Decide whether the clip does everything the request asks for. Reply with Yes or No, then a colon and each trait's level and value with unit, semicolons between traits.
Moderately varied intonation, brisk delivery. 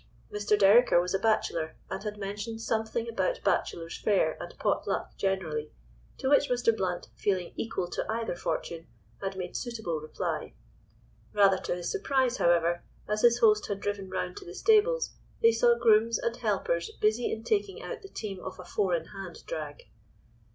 No: average, 4.3 semitones; average, 175 wpm